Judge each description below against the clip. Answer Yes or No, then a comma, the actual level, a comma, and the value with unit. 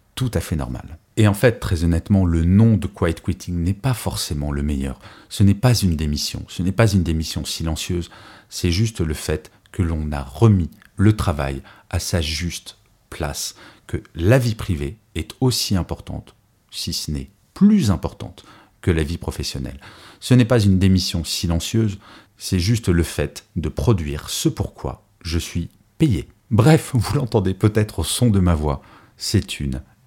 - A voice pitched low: Yes, very low, 95 Hz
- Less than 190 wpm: Yes, average, 175 wpm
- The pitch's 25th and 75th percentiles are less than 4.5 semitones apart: No, average, 4.9 semitones